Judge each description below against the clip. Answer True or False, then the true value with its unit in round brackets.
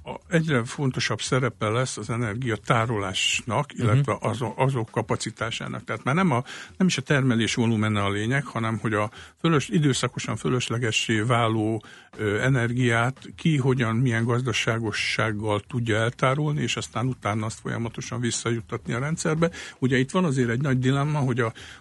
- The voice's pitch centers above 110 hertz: True (120 Hz)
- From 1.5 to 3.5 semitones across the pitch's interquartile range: True (2.7 semitones)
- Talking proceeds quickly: False (145 wpm)